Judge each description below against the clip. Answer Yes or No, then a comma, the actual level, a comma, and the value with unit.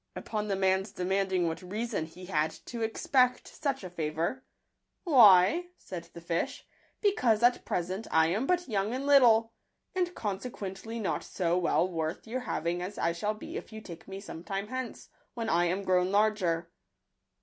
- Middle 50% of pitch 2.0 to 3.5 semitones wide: No, average, 4.6 semitones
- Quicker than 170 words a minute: Yes, average, 185 wpm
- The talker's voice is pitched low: No, high, 195 Hz